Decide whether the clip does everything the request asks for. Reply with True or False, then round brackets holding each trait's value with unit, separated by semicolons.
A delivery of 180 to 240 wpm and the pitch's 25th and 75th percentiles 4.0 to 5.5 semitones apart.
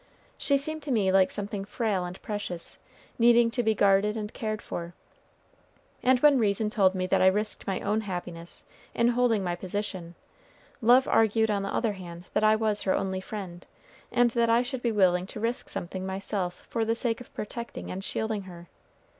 False (190 wpm; 3.5 semitones)